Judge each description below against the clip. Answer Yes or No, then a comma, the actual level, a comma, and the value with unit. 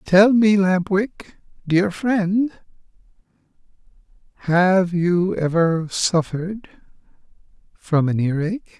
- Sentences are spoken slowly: Yes, slow, 90 wpm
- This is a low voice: No, medium, 185 Hz